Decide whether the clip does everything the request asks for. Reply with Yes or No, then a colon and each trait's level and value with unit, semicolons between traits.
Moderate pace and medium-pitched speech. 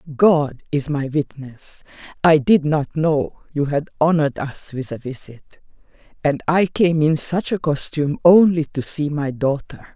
Yes: average, 165 wpm; medium, 150 Hz